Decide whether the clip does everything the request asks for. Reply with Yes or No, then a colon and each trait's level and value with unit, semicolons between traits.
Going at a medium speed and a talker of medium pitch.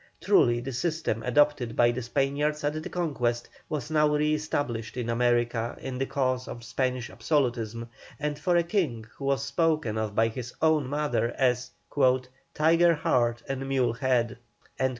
No: average, 160 wpm; low, 130 Hz